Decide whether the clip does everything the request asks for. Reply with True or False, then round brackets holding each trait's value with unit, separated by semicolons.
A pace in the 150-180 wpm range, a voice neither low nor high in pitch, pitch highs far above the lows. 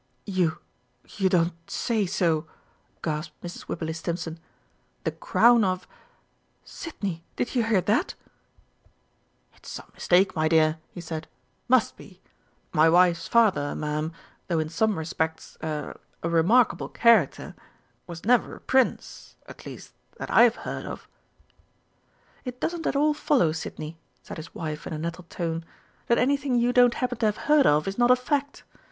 True (155 wpm; 180 Hz; 6.9 semitones)